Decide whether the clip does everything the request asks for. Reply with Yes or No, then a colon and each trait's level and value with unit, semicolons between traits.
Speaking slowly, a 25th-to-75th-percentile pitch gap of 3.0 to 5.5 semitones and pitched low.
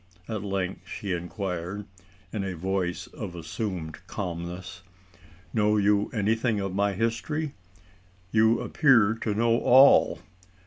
Yes: slow, 120 wpm; average, 3.5 semitones; low, 100 Hz